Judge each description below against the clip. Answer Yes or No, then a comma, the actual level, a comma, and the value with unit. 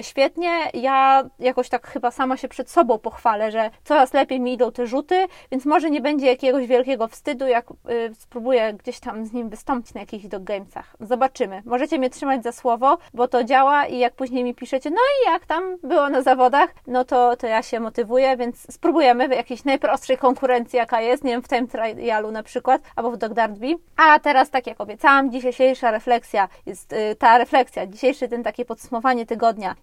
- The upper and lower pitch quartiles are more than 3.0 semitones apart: No, narrow, 2.4 semitones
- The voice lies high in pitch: Yes, very high, 250 Hz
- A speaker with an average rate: No, fast, 195 wpm